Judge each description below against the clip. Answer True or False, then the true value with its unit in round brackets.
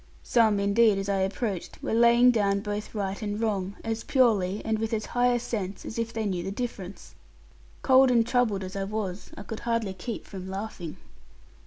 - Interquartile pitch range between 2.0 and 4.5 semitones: True (2.9 semitones)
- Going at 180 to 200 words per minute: True (195 wpm)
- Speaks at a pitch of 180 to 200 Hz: False (215 Hz)